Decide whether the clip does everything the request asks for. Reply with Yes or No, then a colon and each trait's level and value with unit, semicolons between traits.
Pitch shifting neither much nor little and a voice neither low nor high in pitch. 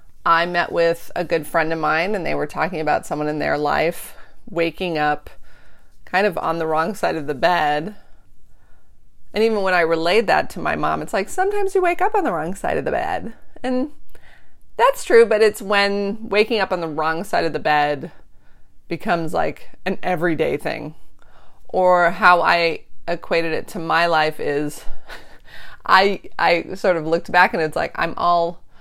Yes: average, 4.3 semitones; medium, 175 Hz